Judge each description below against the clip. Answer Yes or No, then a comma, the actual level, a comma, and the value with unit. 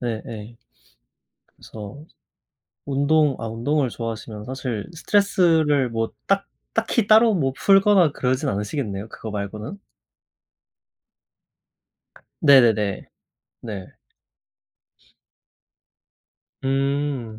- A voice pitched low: Yes, low, 130 Hz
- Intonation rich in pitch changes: Yes, wide, 5.7 semitones